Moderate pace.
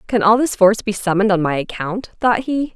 No: fast, 240 wpm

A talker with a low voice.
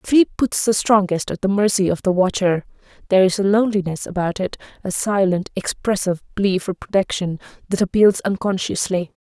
No: high, 190 Hz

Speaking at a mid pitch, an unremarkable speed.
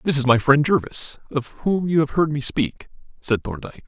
No: medium, 145 Hz; fast, 215 wpm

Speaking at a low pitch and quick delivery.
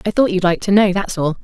No: high, 195 Hz; fast, 335 wpm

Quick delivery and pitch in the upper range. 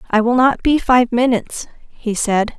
No: average, 185 wpm; high, 240 Hz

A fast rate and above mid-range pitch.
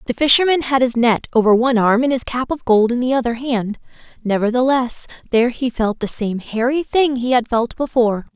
Yes: fast, 210 wpm; high, 245 Hz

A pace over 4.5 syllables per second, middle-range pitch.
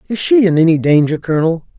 Yes: 6.6 syllables/s; medium, 170 Hz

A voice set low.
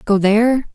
No: high, 220 Hz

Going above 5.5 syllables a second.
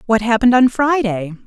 Yes: 5.8 syllables/s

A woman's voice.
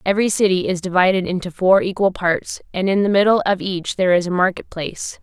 Yes: female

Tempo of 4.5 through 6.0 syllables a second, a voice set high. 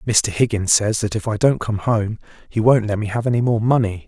No: 5.5 syllables/s; low, 110 Hz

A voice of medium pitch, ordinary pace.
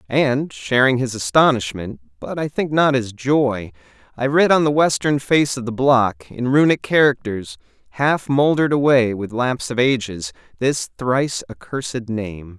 No: low, 125 Hz; average, 155 wpm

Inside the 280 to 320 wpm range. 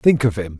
Yes: fast, 300 wpm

